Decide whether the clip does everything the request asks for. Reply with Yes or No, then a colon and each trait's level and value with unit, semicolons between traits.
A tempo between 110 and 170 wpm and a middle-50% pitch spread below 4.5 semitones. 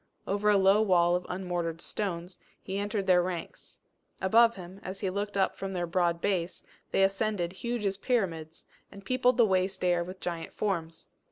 No: average, 180 wpm; narrow, 2.6 semitones